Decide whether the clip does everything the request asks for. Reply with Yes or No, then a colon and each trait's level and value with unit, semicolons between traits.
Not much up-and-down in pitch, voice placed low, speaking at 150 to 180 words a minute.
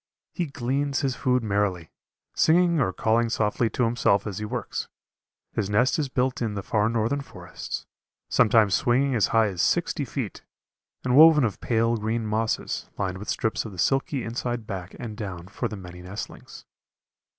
No: average, 3.6 semitones; low, 115 Hz; average, 175 wpm